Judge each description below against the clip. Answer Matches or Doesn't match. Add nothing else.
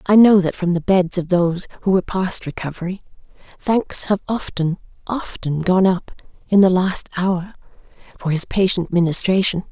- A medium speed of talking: Matches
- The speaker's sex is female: Matches